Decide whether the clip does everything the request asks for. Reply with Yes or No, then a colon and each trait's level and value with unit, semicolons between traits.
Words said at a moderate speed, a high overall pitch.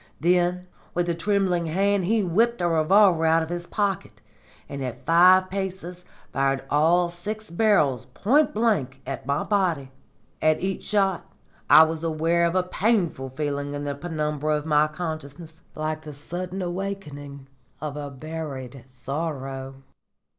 No: average, 145 wpm; medium, 165 Hz